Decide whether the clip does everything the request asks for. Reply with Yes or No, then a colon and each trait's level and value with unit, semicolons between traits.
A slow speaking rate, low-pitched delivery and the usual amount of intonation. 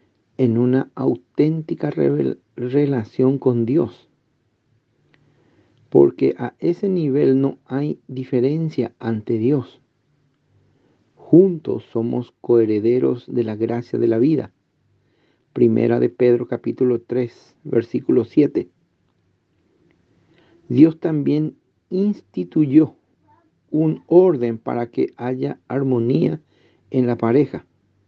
Yes: slow, 95 wpm; low, 125 Hz; average, 3.7 semitones